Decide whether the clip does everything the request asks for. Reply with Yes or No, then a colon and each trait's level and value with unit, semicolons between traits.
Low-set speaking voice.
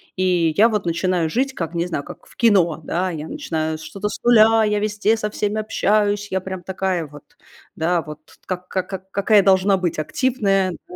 No: high, 190 Hz